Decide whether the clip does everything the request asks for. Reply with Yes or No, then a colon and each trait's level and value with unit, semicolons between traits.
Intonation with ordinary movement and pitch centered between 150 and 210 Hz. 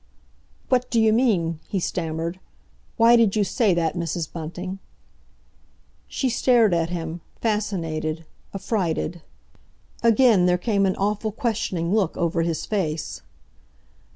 Yes: average, 4.8 semitones; medium, 185 Hz